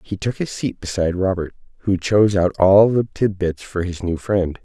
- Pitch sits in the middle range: No, very low, 95 Hz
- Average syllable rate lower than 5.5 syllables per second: Yes, 5.1 syllables/s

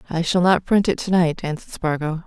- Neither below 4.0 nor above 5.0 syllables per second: No, 5.8 syllables/s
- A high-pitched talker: No, medium, 170 Hz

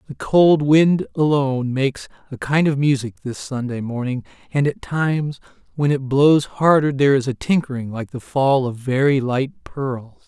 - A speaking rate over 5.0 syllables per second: No, 4.5 syllables/s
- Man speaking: Yes, male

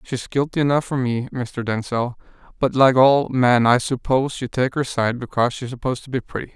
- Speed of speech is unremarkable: No, fast, 230 wpm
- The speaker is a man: Yes, male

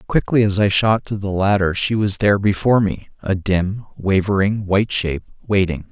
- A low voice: Yes, low, 100 Hz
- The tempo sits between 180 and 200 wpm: Yes, average, 185 wpm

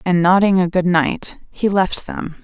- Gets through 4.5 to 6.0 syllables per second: No, 4.0 syllables/s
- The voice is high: No, medium, 180 Hz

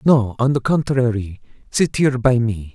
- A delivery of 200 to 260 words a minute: No, average, 175 wpm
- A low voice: Yes, low, 120 Hz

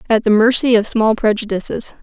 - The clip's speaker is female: Yes, female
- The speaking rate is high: No, average, 180 wpm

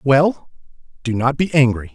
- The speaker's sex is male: Yes, male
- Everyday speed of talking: Yes, average, 155 wpm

